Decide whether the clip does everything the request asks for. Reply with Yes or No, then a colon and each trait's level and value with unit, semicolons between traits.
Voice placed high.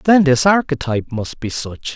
No: medium, 140 Hz